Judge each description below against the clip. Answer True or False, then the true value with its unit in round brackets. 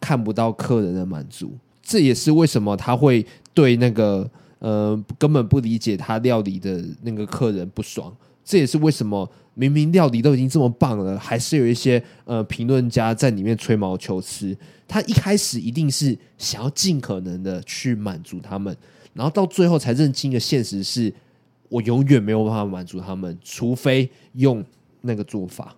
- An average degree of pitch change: True (4.8 semitones)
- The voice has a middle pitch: False (120 Hz)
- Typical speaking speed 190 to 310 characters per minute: True (270 characters per minute)